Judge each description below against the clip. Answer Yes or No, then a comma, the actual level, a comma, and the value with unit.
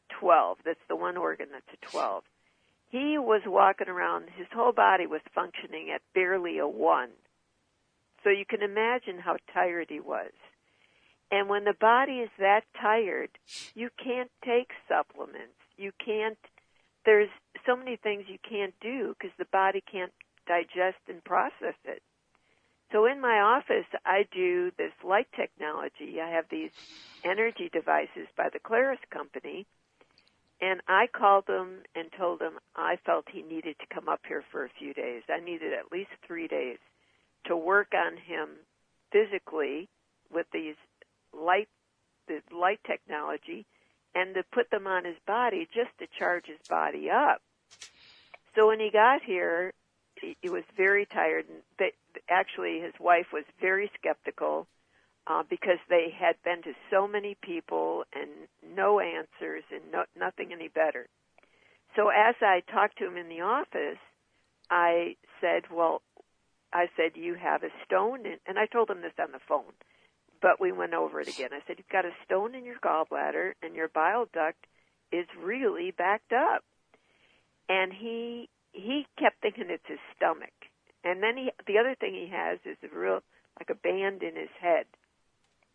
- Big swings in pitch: Yes, wide, 6.0 semitones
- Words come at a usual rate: Yes, average, 165 wpm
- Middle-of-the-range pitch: No, high, 205 Hz